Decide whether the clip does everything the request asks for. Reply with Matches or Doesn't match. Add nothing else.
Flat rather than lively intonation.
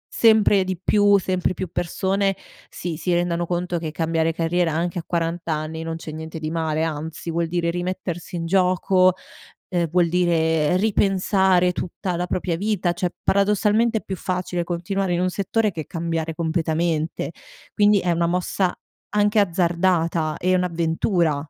Matches